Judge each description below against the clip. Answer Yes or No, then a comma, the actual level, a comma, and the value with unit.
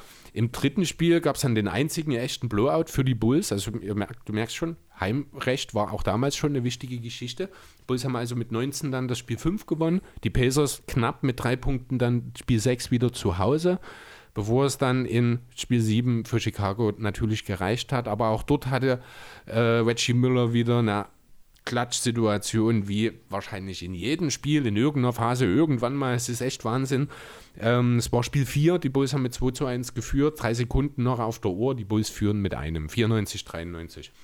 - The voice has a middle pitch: No, low, 120 Hz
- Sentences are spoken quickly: Yes, fast, 195 wpm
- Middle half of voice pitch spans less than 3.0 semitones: No, average, 3.4 semitones